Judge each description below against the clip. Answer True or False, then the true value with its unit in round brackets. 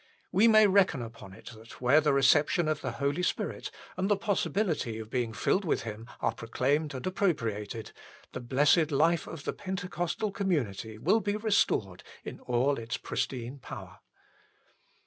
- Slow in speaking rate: False (160 wpm)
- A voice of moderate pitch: True (145 Hz)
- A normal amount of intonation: False (7.9 semitones)